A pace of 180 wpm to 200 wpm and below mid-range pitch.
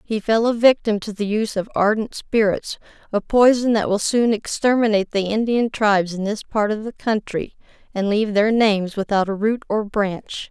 No: average, 190 wpm; high, 215 Hz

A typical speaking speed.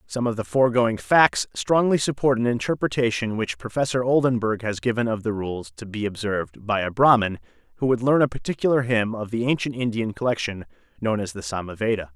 Yes: average, 190 wpm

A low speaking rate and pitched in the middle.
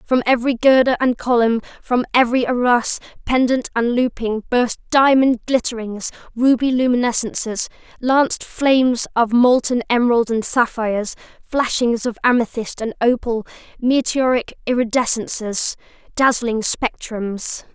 No: slow, 110 wpm; high, 240 Hz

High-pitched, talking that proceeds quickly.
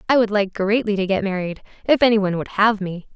Yes: high, 205 Hz; fast, 245 wpm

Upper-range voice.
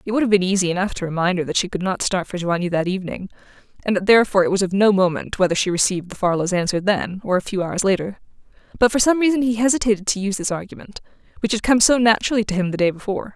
Yes: high, 195 Hz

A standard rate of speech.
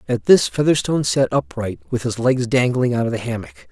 No: fast, 210 wpm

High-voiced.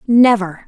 Yes: high, 215 Hz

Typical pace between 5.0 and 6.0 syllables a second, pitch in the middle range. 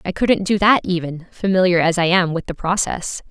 Yes: 5.2 syllables/s; medium, 180 Hz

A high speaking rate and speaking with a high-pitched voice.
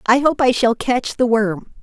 Yes: fast, 230 wpm; high, 240 Hz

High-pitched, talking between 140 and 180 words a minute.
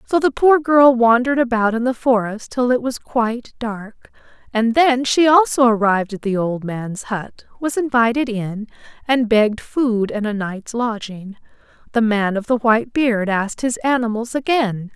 Yes: high, 235 Hz; average, 175 wpm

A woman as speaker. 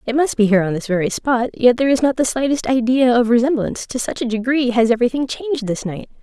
Yes: female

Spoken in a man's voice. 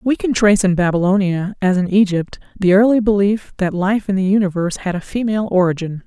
No: female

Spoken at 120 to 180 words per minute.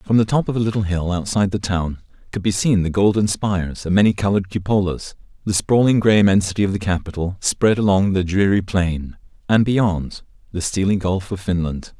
No: average, 195 wpm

